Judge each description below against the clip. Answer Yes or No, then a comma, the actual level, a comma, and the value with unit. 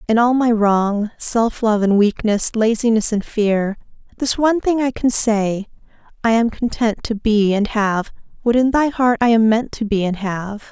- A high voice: Yes, high, 220 Hz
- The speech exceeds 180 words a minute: Yes, average, 195 wpm